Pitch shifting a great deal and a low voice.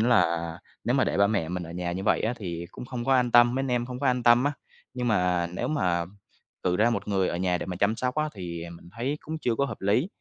Yes: wide, 5.8 semitones; low, 110 Hz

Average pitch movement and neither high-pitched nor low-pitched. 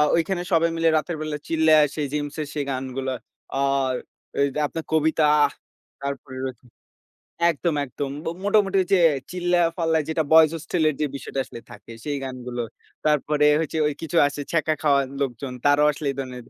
Yes: average, 3.1 semitones; medium, 150 Hz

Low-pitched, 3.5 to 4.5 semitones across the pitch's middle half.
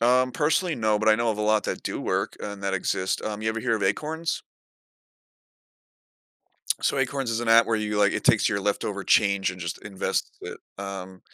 No: low, 110 Hz; average, 3.0 semitones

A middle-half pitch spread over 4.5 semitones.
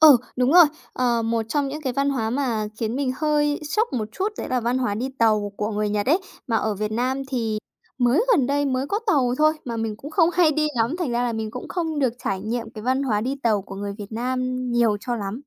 No: average, 4.2 semitones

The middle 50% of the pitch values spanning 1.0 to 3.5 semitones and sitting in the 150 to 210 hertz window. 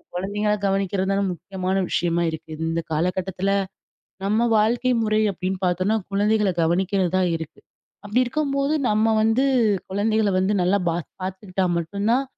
Yes: average, 2.9 semitones; high, 195 Hz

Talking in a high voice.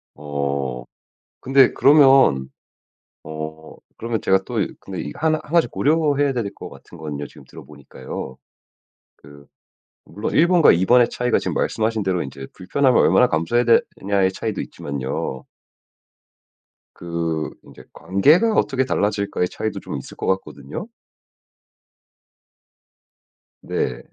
No: very low, 95 Hz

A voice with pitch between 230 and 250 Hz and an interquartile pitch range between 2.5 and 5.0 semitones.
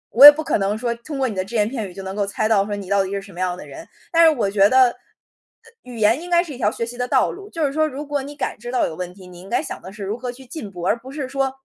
No: high, 235 Hz; wide, 5.6 semitones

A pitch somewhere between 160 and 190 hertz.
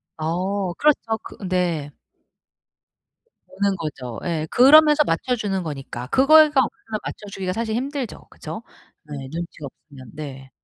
Yes: medium, 185 Hz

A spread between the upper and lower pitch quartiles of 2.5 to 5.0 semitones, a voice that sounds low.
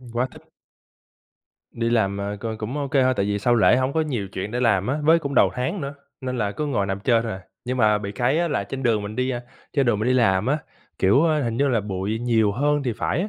Yes: average, 4.5 semitones; low, 120 Hz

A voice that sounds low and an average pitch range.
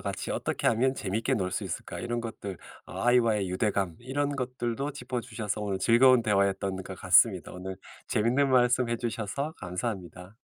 Yes: low, 115 Hz; average, 4.3 semitones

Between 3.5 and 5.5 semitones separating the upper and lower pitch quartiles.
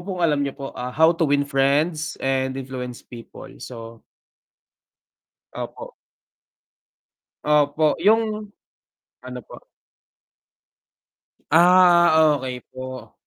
Yes: average, 4.2 semitones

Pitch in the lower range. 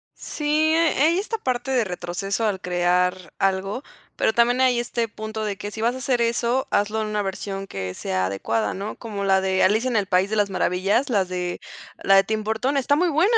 No: high, 210 Hz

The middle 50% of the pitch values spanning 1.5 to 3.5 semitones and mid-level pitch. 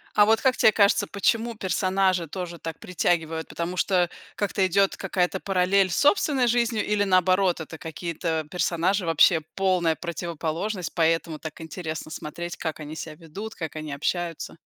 Yes: average, 3.2 semitones; medium, 180 Hz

